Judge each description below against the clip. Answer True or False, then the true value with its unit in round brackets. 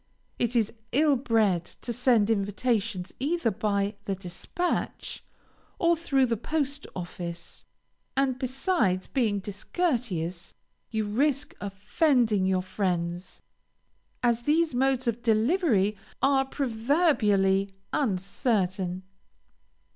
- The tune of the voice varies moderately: False (5.7 semitones)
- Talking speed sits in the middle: False (100 wpm)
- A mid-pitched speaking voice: False (225 Hz)